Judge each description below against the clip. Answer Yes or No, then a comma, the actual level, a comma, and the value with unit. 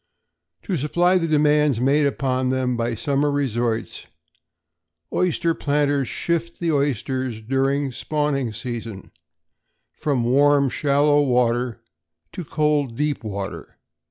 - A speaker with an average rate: No, slow, 115 wpm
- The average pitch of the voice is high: No, medium, 140 Hz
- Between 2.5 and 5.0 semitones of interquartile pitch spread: Yes, average, 3.4 semitones